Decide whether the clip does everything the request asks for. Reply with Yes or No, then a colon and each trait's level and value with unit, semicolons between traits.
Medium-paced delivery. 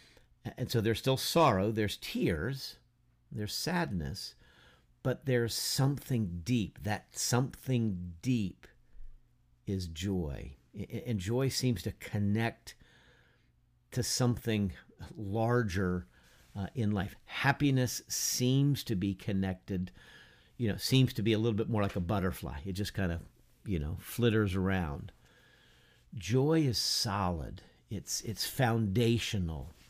No: slow, 120 wpm